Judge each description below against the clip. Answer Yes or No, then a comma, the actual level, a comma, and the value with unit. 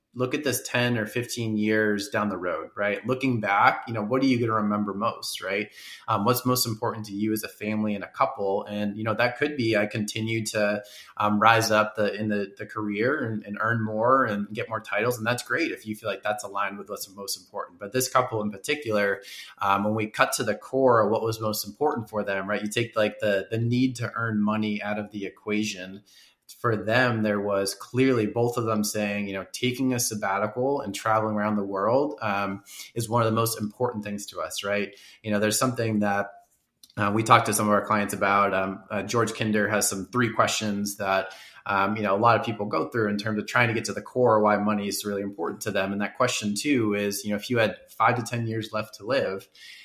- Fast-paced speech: Yes, fast, 240 wpm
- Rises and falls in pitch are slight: Yes, narrow, 2.2 semitones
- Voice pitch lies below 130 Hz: Yes, low, 105 Hz